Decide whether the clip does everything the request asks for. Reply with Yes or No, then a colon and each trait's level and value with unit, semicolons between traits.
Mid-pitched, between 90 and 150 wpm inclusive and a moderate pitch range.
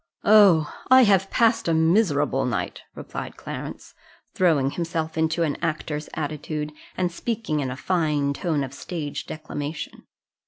Yes: medium, 160 Hz; slow, 135 wpm; average, 3.3 semitones